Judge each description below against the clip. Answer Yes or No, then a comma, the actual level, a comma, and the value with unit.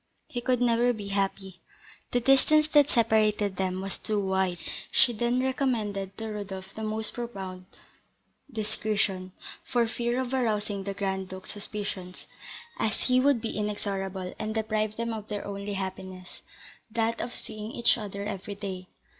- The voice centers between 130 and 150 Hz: No, high, 210 Hz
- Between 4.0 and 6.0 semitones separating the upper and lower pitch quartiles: No, average, 3.2 semitones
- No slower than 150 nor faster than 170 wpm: Yes, average, 155 wpm